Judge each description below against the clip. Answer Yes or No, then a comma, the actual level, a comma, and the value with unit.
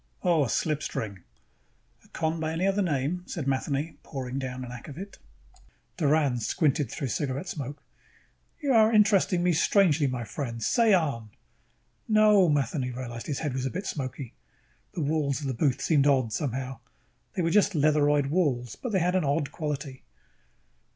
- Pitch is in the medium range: Yes, medium, 145 Hz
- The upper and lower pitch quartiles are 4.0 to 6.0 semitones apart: Yes, average, 4.7 semitones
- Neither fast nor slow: Yes, average, 165 wpm